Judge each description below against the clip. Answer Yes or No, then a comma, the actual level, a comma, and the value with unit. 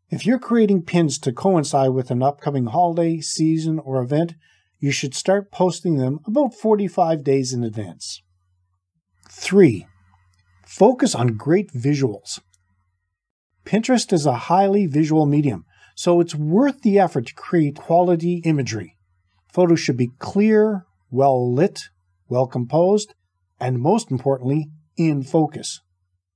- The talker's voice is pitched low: No, medium, 145 Hz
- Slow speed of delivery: Yes, slow, 125 wpm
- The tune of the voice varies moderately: No, wide, 8.8 semitones